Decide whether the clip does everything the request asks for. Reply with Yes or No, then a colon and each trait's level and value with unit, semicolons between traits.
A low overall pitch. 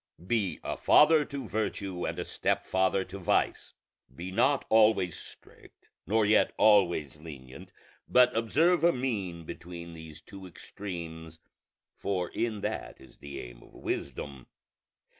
Yes: very low, 95 Hz